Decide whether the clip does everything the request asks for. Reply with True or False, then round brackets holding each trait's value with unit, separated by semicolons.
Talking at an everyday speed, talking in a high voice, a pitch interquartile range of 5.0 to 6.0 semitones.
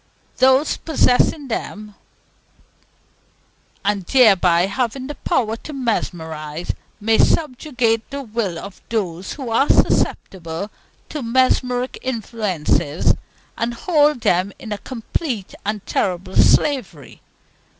False (105 wpm; 225 Hz; 5.5 semitones)